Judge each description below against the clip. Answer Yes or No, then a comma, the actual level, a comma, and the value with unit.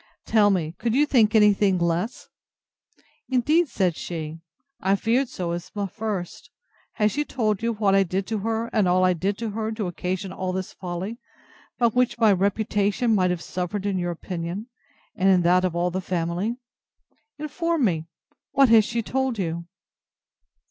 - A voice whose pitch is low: No, high, 200 Hz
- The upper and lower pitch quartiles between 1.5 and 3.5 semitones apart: No, average, 4.1 semitones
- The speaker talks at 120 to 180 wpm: Yes, average, 170 wpm